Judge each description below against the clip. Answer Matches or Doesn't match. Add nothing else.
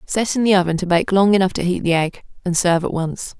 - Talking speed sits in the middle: Doesn't match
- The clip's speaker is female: Matches